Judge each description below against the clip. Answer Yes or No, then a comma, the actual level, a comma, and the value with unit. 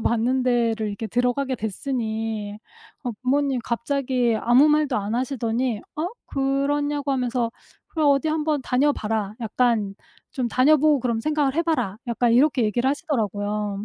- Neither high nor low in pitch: No, very high, 250 Hz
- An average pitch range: Yes, average, 3.8 semitones